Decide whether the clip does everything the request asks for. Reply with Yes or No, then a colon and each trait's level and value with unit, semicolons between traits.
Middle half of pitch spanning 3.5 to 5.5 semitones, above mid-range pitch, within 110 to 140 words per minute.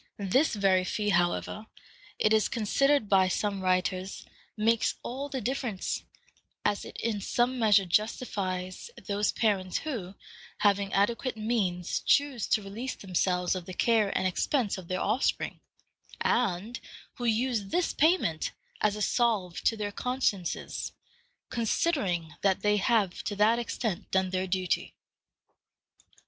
Yes: average, 4.0 semitones; high, 205 Hz; slow, 135 wpm